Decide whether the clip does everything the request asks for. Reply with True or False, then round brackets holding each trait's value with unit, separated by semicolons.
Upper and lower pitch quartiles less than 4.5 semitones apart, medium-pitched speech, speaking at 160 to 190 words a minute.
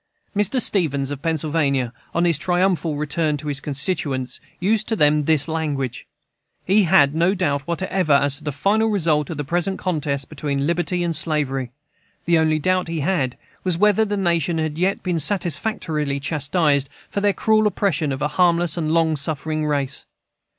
True (3.9 semitones; 160 Hz; 170 wpm)